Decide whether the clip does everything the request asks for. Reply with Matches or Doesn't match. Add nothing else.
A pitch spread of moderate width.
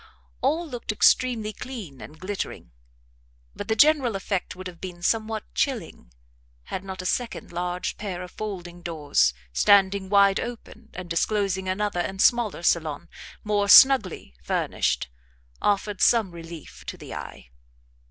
Matches